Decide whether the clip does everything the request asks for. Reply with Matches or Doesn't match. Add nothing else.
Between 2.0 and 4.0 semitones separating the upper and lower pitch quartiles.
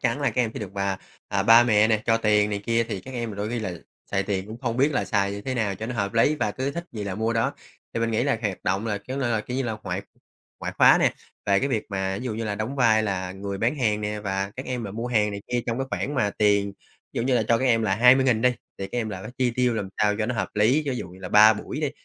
Matches